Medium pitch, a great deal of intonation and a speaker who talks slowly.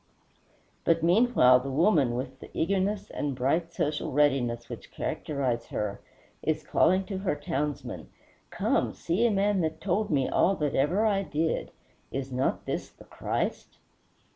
No: medium, 155 Hz; wide, 6.1 semitones; average, 150 wpm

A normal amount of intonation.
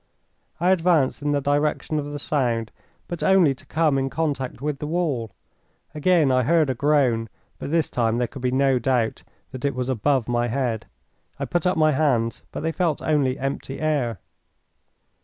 Yes: average, 3.5 semitones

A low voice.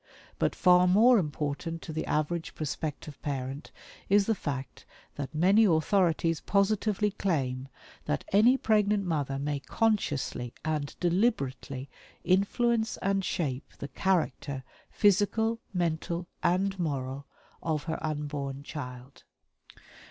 No: medium, 165 Hz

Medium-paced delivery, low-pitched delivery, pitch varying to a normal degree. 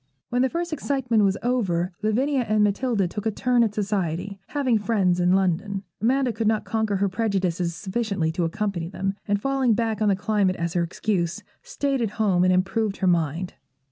No: average, 190 wpm; high, 205 Hz; average, 3.9 semitones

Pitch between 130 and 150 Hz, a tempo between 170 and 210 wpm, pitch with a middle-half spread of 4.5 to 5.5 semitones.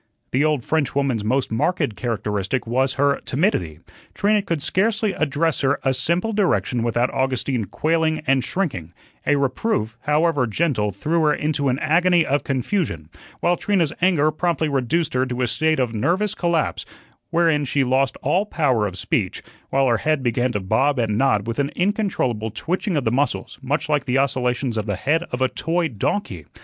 Yes: medium, 140 Hz; average, 180 wpm; average, 5.2 semitones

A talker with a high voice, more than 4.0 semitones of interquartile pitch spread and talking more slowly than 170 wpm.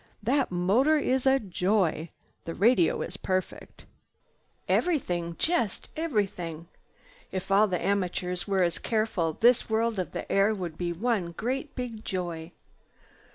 Yes: high, 195 Hz; average, 4.9 semitones; slow, 135 wpm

